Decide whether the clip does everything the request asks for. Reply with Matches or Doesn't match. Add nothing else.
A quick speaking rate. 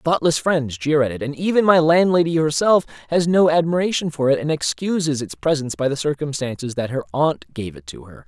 Matches